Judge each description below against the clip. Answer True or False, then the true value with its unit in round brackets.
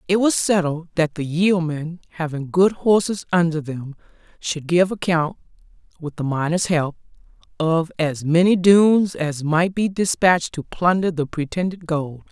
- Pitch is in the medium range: True (170 Hz)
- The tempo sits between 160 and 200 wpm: False (150 wpm)